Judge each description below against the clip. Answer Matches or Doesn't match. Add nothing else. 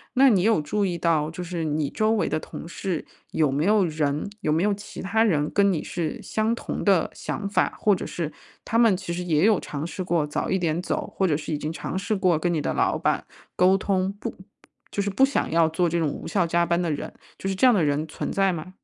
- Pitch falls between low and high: Matches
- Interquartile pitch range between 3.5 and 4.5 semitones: Matches